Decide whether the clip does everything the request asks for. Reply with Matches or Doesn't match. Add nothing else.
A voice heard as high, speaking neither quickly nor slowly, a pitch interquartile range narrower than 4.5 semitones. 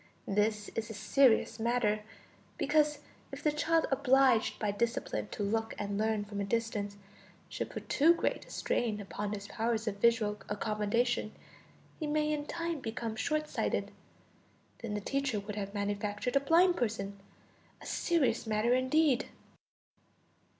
Doesn't match